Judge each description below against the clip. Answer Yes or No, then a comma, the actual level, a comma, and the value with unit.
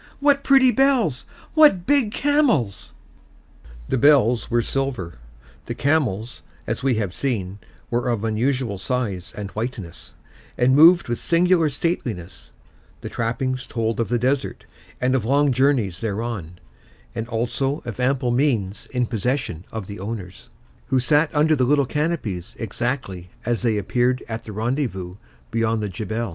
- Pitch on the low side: Yes, low, 120 Hz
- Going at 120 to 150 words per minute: Yes, average, 145 wpm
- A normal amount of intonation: Yes, average, 4.6 semitones